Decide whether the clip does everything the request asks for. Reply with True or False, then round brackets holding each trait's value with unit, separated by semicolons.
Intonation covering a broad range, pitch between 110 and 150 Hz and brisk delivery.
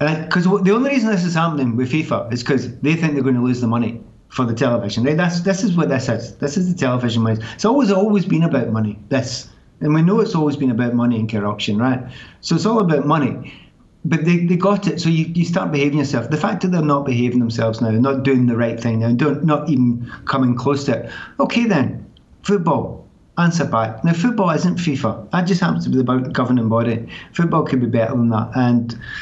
True (6.1 semitones; 135 Hz; 235 wpm)